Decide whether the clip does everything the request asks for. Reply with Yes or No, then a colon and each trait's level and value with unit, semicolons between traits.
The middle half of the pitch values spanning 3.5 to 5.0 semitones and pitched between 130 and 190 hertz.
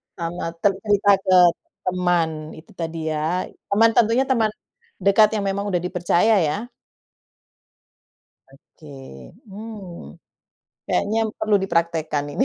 Yes: average, 4.0 semitones; medium, 185 Hz